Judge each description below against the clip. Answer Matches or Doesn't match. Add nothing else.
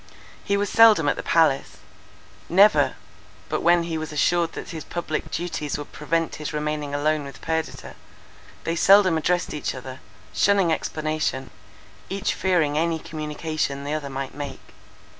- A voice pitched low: Doesn't match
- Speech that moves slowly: Doesn't match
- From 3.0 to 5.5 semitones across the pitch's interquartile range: Doesn't match